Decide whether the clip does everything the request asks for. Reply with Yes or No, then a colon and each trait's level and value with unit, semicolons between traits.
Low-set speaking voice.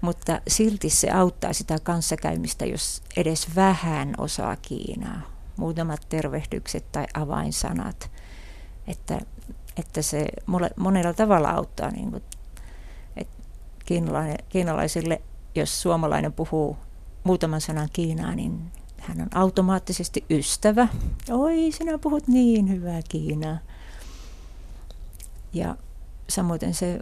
No: medium, 160 Hz